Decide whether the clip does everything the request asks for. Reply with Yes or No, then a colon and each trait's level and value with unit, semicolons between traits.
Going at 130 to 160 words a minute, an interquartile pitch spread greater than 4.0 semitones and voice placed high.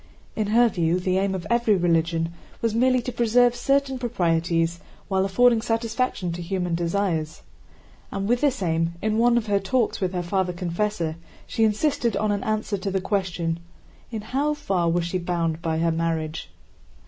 No: average, 175 wpm; average, 5.1 semitones; high, 195 Hz